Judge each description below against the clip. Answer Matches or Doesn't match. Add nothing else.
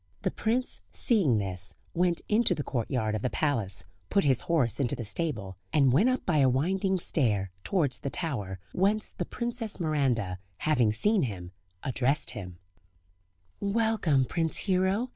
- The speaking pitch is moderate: Matches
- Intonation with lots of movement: Matches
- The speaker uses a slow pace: Doesn't match